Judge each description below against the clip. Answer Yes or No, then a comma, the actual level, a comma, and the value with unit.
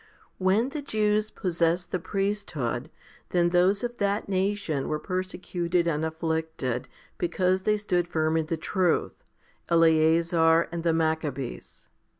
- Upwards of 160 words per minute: No, slow, 135 wpm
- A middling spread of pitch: Yes, average, 3.2 semitones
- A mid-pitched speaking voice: Yes, medium, 175 Hz